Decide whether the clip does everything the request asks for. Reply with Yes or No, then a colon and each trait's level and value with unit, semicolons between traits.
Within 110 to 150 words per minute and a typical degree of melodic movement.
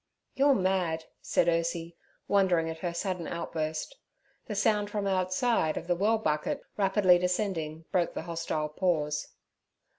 Yes: average, 140 wpm; average, 3.5 semitones